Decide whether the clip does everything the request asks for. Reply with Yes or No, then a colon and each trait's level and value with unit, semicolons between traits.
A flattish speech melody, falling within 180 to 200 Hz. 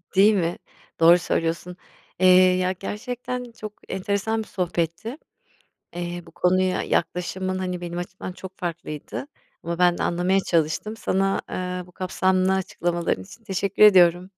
Yes: narrow, 1.8 semitones; medium, 185 Hz